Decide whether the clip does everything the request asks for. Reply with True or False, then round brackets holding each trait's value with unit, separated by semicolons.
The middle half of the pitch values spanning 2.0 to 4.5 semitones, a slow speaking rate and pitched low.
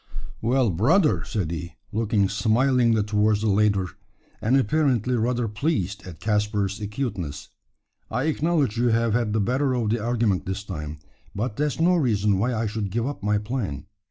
False (3.6 semitones; 165 wpm; 110 Hz)